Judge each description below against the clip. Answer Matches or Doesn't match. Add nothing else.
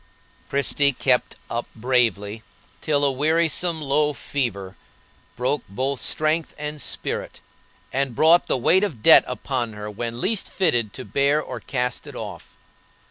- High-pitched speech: Doesn't match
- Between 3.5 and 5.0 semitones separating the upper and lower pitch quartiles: Matches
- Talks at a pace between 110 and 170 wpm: Matches